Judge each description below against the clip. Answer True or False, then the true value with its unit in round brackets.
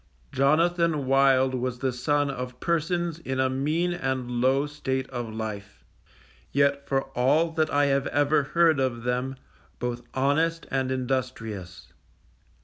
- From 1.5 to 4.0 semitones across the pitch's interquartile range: True (2.8 semitones)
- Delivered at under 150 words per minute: True (140 wpm)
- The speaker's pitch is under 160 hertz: True (135 Hz)